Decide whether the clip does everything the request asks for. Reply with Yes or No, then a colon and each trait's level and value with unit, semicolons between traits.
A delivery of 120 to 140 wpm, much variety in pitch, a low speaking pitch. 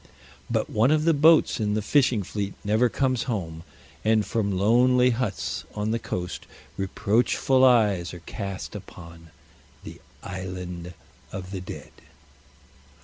No: slow, 135 wpm; average, 5.0 semitones; low, 105 Hz